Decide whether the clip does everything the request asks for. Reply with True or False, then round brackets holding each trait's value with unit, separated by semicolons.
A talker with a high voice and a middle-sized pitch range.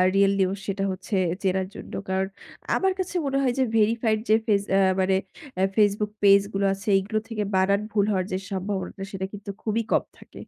False (200 Hz; 2.1 semitones)